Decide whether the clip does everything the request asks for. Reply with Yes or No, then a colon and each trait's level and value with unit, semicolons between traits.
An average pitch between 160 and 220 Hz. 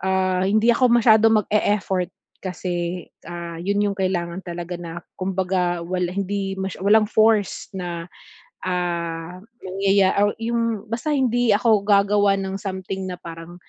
Yes: high, 190 Hz